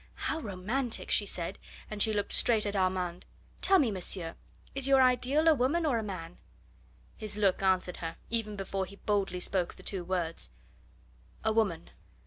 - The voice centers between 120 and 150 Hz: No, high, 205 Hz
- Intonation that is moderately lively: Yes, average, 4.5 semitones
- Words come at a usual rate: Yes, average, 170 wpm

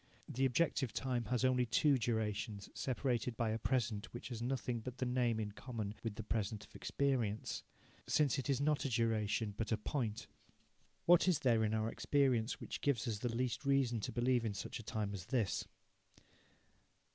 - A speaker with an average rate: Yes, average, 185 wpm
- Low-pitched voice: Yes, low, 120 Hz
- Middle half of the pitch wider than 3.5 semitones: No, average, 2.9 semitones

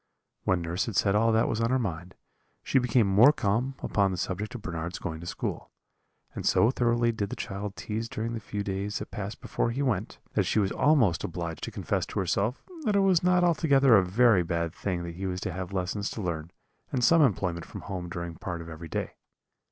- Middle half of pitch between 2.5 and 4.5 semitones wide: No, average, 4.9 semitones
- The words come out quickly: Yes, fast, 225 wpm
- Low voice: Yes, low, 100 Hz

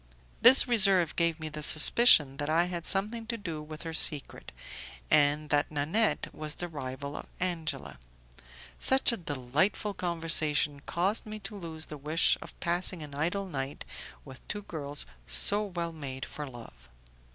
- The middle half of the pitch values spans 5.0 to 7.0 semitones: No, average, 4.2 semitones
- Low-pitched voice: No, medium, 160 Hz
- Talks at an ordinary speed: Yes, average, 160 wpm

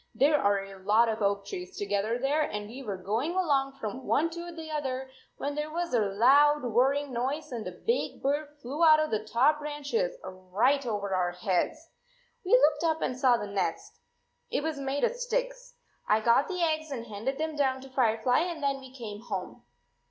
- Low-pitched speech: No, very high, 270 Hz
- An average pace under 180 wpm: No, fast, 205 wpm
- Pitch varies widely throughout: Yes, wide, 6.0 semitones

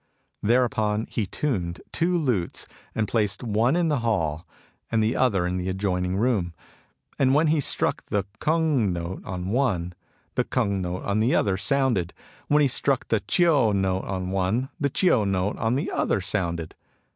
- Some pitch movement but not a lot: No, wide, 5.8 semitones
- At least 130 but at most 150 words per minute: No, average, 170 wpm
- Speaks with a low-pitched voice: Yes, low, 105 Hz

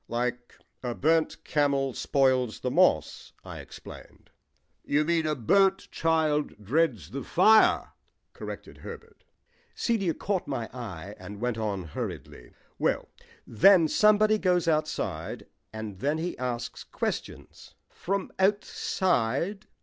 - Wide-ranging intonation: Yes, wide, 7.2 semitones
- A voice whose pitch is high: No, medium, 145 Hz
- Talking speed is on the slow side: Yes, slow, 120 wpm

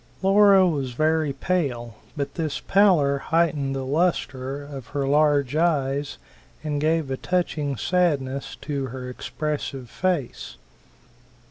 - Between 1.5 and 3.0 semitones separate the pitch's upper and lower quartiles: No, average, 3.4 semitones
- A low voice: No, medium, 145 Hz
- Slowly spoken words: Yes, slow, 120 wpm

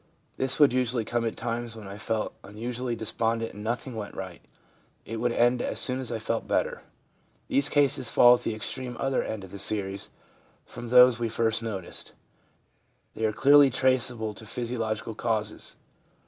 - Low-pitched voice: Yes, low, 115 Hz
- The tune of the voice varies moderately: No, narrow, 2.3 semitones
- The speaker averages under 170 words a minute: No, average, 175 wpm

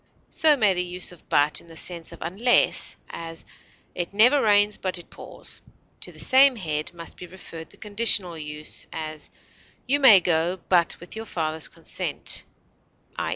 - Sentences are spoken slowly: No, average, 170 wpm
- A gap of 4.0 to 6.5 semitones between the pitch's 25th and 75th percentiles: Yes, average, 4.3 semitones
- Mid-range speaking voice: Yes, medium, 180 Hz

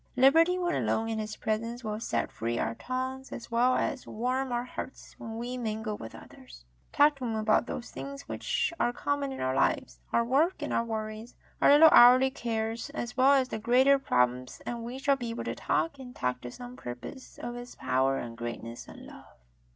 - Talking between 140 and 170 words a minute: No, fast, 205 wpm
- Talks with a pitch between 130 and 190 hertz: No, high, 240 Hz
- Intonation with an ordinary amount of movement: Yes, average, 3.6 semitones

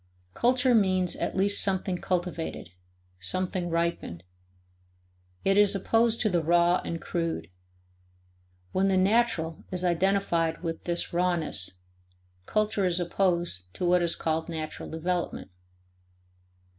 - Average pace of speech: No, slow, 120 wpm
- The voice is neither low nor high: Yes, medium, 175 Hz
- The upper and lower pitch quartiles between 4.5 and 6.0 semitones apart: No, average, 2.7 semitones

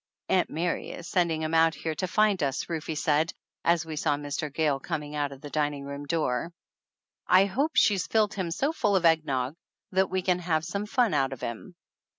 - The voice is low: No, medium, 160 Hz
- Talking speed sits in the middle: No, fast, 210 wpm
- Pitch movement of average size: Yes, average, 4.0 semitones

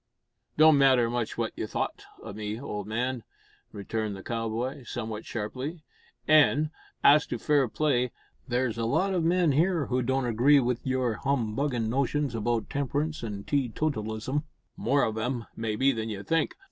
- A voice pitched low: Yes, low, 125 Hz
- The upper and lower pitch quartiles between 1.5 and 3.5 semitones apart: No, average, 4.3 semitones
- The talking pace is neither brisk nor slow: Yes, average, 165 wpm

